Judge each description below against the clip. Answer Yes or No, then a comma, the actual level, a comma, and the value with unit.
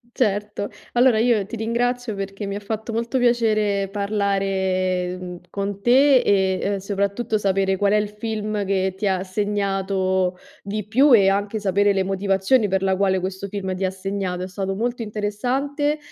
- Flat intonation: Yes, narrow, 2.2 semitones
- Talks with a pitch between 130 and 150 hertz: No, high, 200 Hz